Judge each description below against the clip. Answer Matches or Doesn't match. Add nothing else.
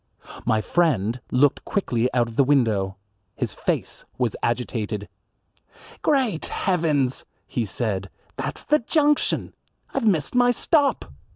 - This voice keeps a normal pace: Doesn't match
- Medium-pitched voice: Doesn't match